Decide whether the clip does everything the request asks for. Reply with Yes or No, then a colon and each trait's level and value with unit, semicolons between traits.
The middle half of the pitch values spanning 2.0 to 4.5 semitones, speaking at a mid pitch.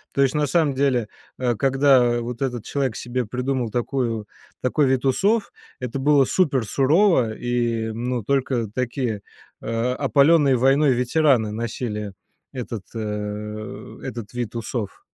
No: average, 3.1 semitones; low, 125 Hz